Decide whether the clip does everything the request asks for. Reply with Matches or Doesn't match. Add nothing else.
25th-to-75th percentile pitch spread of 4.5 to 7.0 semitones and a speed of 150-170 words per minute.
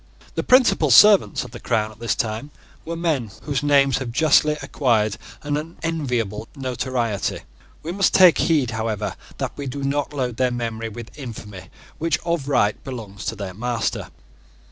Matches